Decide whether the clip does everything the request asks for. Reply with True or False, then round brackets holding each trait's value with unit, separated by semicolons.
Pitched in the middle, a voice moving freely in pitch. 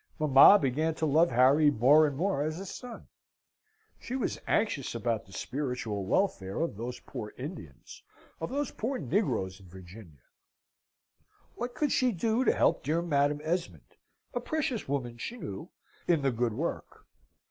True (145 Hz; 8.0 semitones)